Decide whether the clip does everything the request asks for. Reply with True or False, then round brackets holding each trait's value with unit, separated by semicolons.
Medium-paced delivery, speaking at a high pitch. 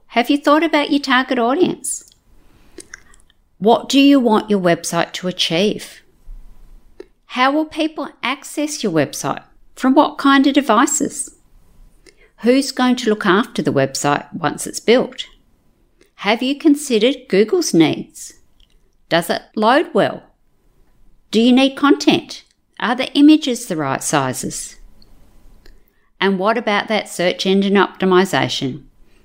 False (125 wpm; 240 Hz)